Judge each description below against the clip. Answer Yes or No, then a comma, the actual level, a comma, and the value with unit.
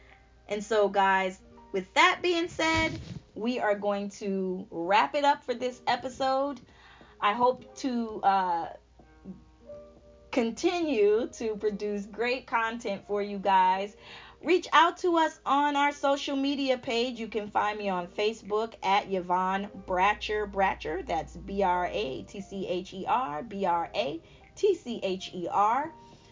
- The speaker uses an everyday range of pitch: No, wide, 5.9 semitones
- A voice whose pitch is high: Yes, high, 215 Hz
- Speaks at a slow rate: Yes, slow, 115 wpm